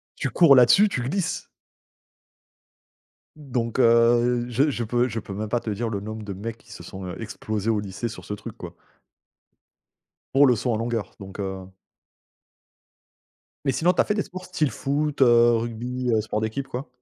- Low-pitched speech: Yes, low, 120 Hz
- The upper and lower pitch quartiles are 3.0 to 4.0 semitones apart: Yes, average, 3.5 semitones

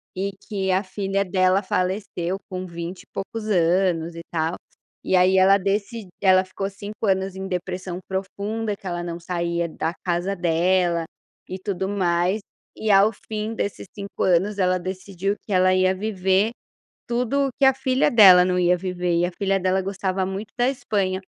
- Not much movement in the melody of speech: Yes, narrow, 1.8 semitones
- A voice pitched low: No, high, 190 Hz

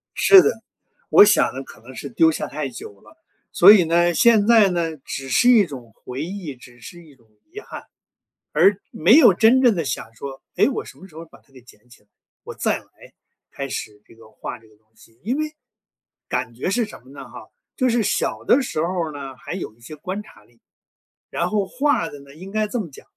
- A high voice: No, medium, 160 Hz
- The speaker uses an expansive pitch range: Yes, wide, 8.3 semitones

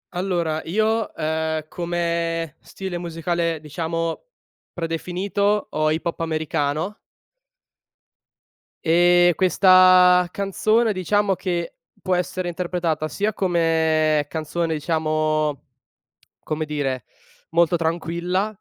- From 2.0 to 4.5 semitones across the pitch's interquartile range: Yes, narrow, 2.5 semitones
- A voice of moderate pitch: Yes, medium, 170 Hz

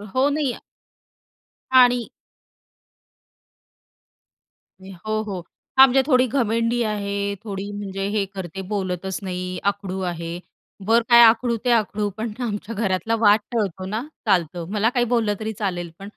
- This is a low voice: No, high, 210 Hz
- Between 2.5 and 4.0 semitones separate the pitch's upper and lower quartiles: Yes, average, 3.3 semitones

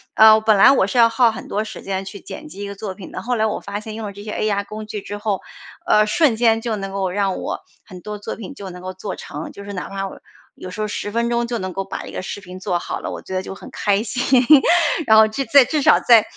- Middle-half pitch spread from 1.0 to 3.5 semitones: Yes, narrow, 2.4 semitones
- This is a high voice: Yes, high, 210 Hz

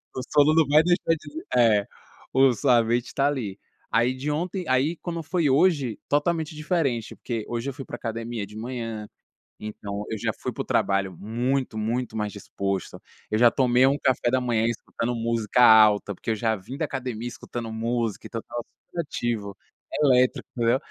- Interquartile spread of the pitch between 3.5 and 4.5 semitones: Yes, average, 3.8 semitones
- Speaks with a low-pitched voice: Yes, low, 120 Hz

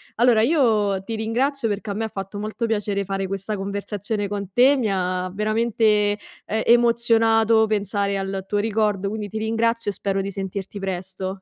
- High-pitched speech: Yes, high, 210 Hz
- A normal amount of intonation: No, narrow, 2.3 semitones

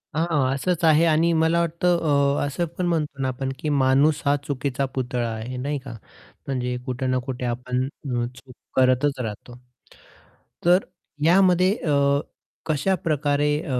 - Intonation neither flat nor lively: Yes, average, 4.0 semitones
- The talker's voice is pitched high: No, medium, 140 Hz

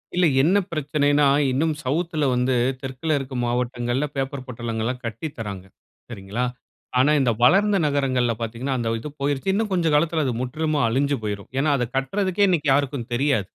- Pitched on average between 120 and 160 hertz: Yes, low, 135 Hz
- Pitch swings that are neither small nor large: Yes, average, 3.9 semitones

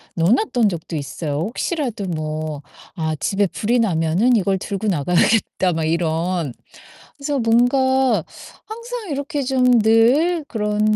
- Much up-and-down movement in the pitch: Yes, wide, 7.7 semitones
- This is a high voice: Yes, high, 210 Hz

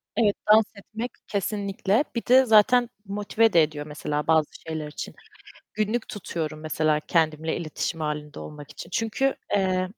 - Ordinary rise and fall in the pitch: No, wide, 5.8 semitones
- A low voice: No, medium, 185 Hz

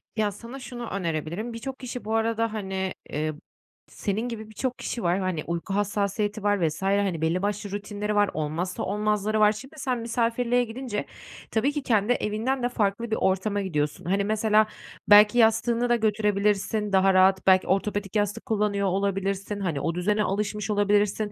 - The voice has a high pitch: Yes, high, 210 Hz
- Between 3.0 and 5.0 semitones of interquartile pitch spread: No, narrow, 2.4 semitones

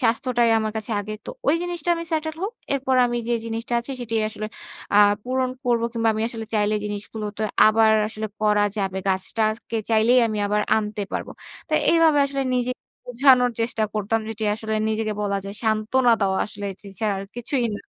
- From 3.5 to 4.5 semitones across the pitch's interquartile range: No, narrow, 2.6 semitones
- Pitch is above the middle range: Yes, high, 225 Hz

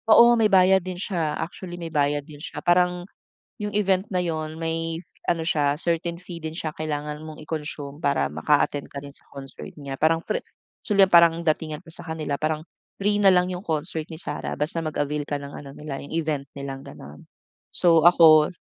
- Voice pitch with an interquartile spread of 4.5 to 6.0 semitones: No, average, 3.0 semitones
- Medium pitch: Yes, medium, 160 Hz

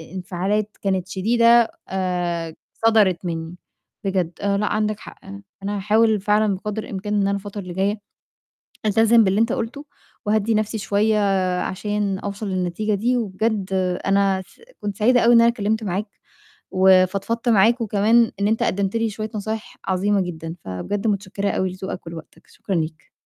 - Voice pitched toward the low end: No, high, 205 Hz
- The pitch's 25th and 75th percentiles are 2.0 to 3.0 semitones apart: Yes, narrow, 2.5 semitones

